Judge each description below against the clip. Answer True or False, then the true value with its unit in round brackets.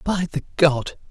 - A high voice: False (155 Hz)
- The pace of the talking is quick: False (165 wpm)